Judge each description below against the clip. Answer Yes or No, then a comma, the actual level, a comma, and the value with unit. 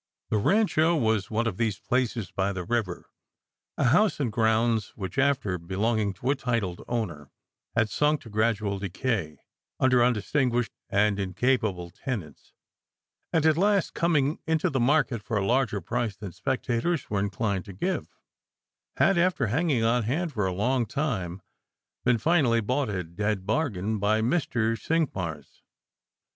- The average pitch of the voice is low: Yes, low, 115 Hz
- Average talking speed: Yes, average, 150 wpm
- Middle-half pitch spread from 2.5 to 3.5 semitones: No, average, 5.0 semitones